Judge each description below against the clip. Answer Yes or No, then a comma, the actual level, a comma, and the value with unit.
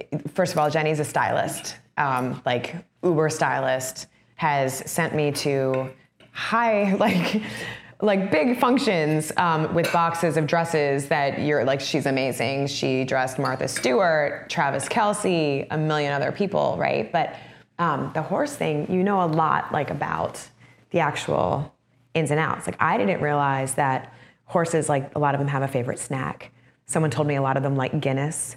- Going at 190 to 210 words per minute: No, average, 170 wpm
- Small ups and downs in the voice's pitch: No, average, 3.5 semitones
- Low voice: No, medium, 150 Hz